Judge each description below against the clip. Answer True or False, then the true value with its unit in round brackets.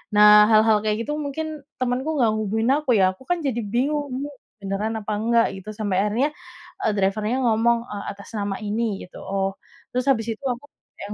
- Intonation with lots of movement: False (3.6 semitones)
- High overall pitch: True (220 Hz)